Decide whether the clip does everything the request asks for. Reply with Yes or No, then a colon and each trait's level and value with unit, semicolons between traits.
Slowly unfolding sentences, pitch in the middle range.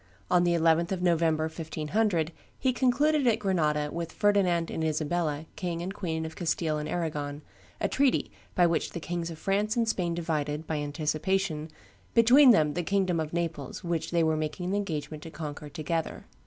No: average, 180 wpm; medium, 165 Hz